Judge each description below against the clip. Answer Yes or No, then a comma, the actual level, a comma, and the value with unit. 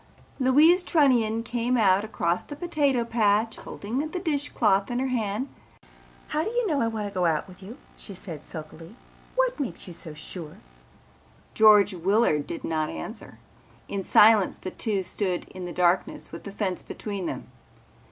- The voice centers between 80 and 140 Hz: No, high, 210 Hz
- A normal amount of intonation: No, wide, 5.7 semitones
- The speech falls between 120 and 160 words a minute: No, average, 170 wpm